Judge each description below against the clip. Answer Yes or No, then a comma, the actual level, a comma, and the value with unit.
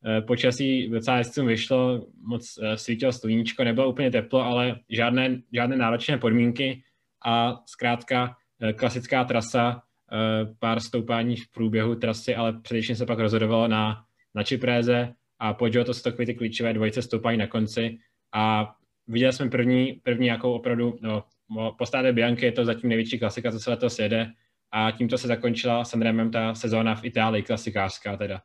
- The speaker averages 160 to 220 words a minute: No, average, 150 wpm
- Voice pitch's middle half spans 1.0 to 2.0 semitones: Yes, narrow, 1.6 semitones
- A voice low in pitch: Yes, low, 120 Hz